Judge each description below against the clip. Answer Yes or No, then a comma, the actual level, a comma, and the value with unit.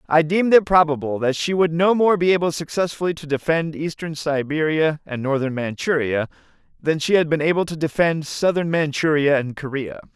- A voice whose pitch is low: No, medium, 155 Hz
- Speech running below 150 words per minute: No, average, 175 wpm